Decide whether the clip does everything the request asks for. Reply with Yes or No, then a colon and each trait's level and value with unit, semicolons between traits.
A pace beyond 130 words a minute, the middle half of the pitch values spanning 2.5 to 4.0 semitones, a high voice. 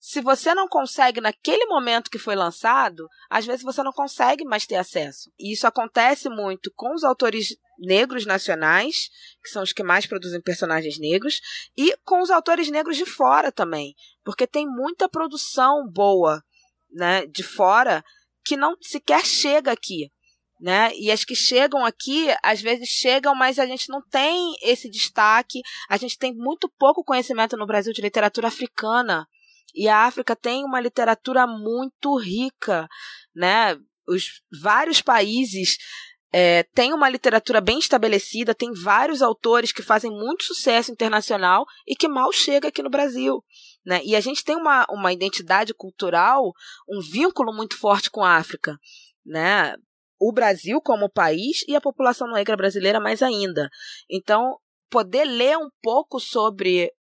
No: average, 155 wpm; wide, 5.4 semitones; high, 240 Hz